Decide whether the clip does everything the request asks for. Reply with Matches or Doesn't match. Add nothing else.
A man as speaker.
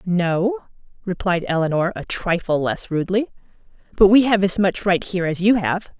Doesn't match